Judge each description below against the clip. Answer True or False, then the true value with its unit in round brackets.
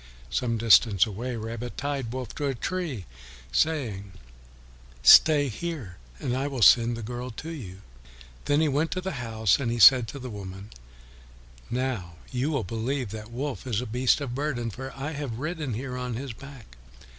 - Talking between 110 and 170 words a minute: False (180 wpm)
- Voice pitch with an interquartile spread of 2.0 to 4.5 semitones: True (3.9 semitones)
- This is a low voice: True (125 Hz)